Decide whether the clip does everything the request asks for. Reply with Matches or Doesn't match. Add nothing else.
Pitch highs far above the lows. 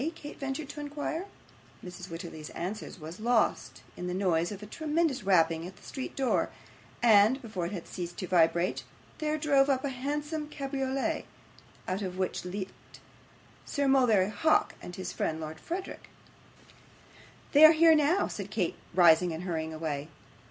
Matches